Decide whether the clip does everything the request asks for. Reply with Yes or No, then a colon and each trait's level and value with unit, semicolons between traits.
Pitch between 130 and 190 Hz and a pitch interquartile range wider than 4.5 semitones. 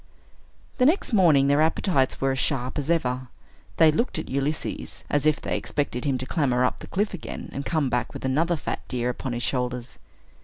No: medium, 140 Hz; average, 3.9 semitones